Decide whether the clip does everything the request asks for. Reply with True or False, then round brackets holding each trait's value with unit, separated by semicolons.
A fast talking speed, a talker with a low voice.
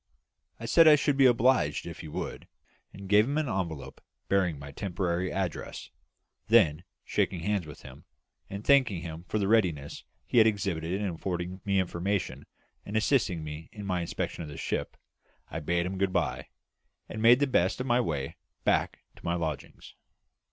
False (180 wpm; 95 Hz)